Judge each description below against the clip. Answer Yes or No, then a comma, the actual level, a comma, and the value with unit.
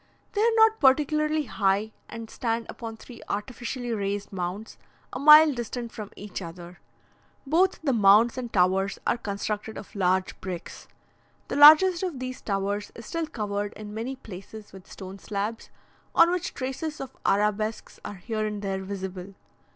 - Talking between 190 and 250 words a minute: No, average, 160 wpm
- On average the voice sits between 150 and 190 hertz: No, high, 220 Hz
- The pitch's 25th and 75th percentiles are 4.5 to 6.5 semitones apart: Yes, average, 5.0 semitones